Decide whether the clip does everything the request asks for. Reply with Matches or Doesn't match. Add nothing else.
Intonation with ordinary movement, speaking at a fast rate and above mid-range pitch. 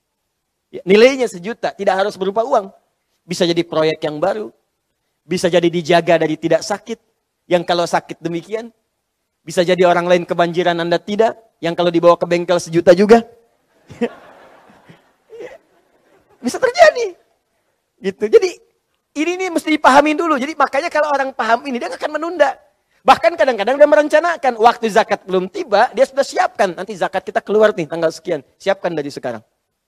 Doesn't match